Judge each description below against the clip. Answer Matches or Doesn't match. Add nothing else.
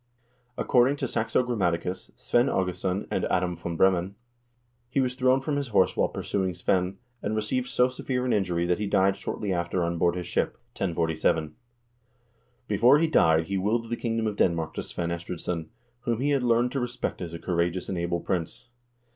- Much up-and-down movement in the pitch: Matches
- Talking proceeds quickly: Doesn't match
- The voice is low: Matches